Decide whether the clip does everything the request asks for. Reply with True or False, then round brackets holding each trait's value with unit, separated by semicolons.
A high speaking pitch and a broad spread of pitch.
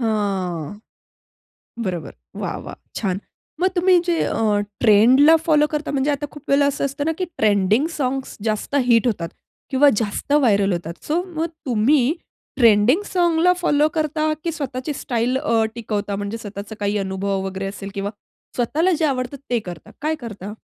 True (235 Hz; 6.4 semitones)